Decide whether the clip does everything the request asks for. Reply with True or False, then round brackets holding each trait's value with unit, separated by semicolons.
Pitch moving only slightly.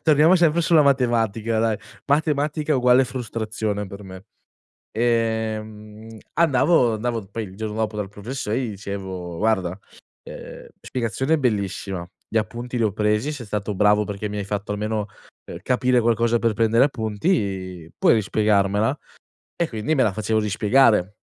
False (3.2 semitones)